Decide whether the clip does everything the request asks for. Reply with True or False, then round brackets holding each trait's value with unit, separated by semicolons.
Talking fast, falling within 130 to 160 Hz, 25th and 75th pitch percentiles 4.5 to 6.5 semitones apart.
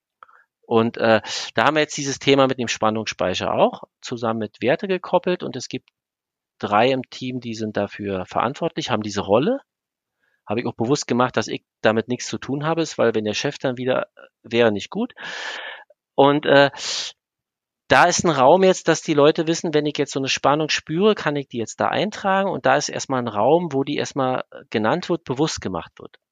True (205 wpm; 135 Hz; 5.6 semitones)